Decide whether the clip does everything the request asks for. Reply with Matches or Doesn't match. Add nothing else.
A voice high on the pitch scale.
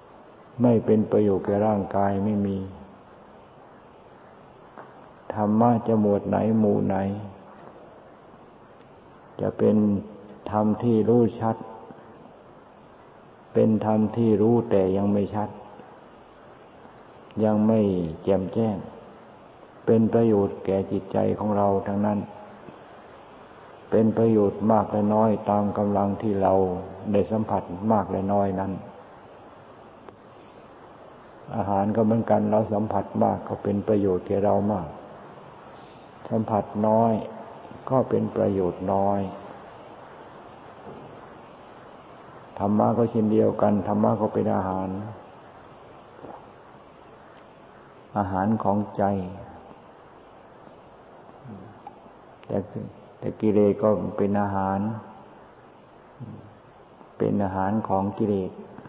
Doesn't match